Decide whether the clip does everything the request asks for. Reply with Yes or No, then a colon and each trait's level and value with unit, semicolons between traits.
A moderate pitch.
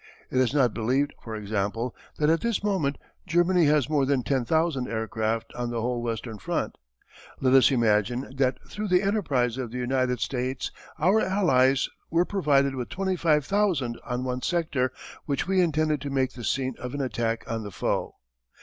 No: low, 130 Hz